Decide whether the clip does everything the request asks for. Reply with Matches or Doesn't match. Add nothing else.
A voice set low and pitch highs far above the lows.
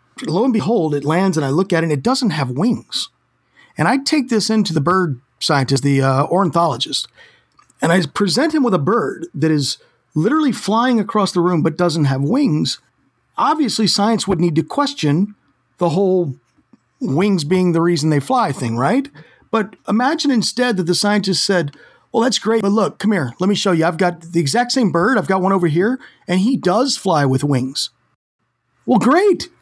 Doesn't match